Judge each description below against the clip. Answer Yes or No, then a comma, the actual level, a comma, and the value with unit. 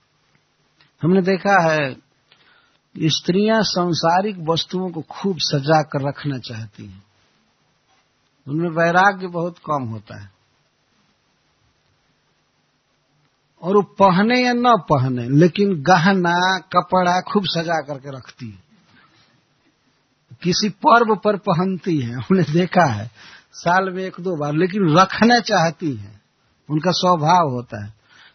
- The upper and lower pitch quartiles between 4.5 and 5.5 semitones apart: Yes, average, 5.1 semitones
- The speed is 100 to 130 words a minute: Yes, average, 115 wpm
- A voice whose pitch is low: No, medium, 170 Hz